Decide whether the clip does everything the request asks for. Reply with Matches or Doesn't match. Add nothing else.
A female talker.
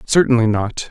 Doesn't match